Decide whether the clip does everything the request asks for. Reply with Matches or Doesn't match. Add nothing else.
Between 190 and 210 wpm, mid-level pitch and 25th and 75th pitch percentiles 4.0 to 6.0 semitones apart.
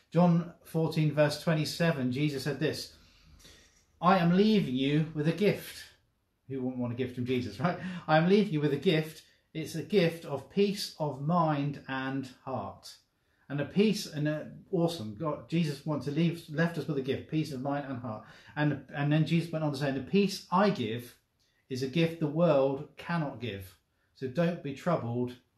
Matches